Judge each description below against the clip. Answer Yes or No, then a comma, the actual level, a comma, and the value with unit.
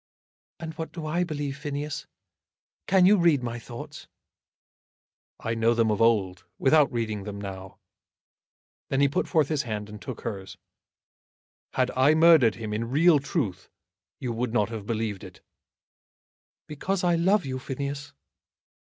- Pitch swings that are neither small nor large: No, wide, 5.8 semitones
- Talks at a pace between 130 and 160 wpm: Yes, average, 150 wpm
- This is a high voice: No, low, 130 Hz